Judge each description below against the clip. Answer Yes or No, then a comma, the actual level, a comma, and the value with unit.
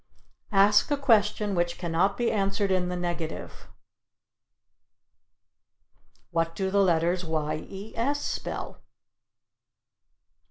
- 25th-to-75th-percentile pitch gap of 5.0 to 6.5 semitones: No, average, 3.1 semitones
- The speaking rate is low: Yes, slow, 105 wpm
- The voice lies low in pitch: No, high, 190 Hz